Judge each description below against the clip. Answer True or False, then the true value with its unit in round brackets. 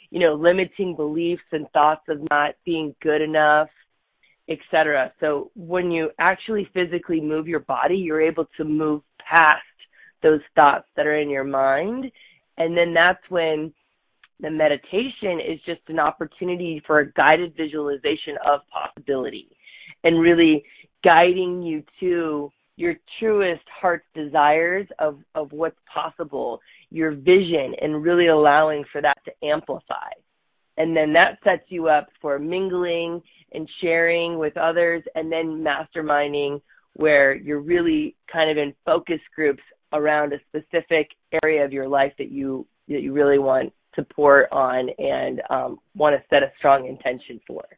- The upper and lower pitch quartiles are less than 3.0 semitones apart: True (2.4 semitones)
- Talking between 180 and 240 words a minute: False (150 wpm)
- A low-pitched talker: False (155 Hz)